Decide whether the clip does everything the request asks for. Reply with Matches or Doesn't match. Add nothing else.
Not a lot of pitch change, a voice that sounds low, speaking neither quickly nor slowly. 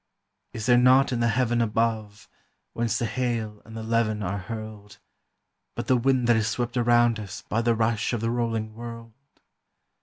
Matches